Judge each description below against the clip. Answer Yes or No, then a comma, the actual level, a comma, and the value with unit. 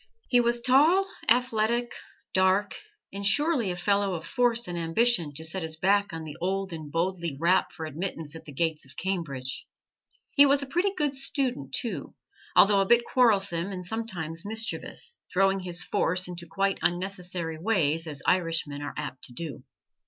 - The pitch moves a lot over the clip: Yes, wide, 5.8 semitones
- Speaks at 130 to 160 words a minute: No, average, 170 wpm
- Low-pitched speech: No, medium, 185 Hz